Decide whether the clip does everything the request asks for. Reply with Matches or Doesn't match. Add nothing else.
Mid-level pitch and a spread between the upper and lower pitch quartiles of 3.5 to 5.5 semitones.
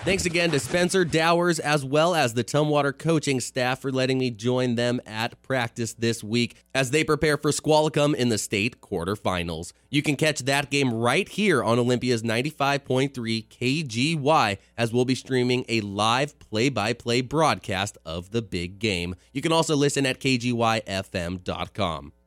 Doesn't match